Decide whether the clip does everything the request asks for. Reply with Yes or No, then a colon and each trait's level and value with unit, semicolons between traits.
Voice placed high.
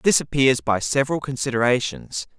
No: low, 125 Hz